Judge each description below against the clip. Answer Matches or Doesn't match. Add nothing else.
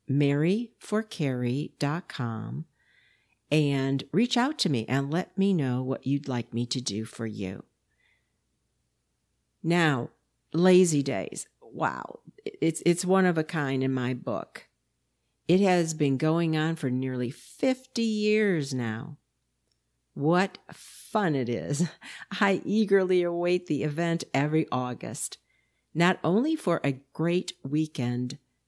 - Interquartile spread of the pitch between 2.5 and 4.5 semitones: Doesn't match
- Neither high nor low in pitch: Matches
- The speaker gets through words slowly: Matches